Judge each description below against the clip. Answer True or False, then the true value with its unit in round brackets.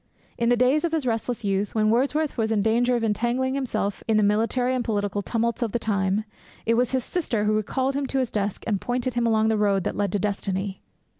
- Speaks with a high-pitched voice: True (225 Hz)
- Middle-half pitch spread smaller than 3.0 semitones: False (3.3 semitones)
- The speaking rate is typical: False (235 wpm)